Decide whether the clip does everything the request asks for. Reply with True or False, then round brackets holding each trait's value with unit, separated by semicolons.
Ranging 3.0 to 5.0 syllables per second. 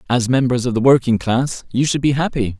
False (5.5 syllables/s)